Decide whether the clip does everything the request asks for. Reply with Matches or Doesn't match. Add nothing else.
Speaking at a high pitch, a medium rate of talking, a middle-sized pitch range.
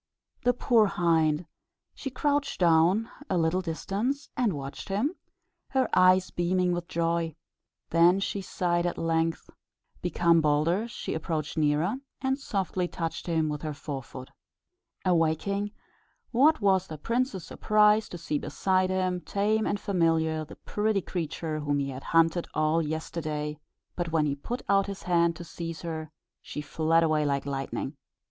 Doesn't match